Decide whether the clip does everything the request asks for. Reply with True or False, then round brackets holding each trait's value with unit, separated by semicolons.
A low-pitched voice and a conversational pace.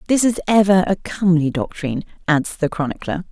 False (175 Hz; 165 wpm)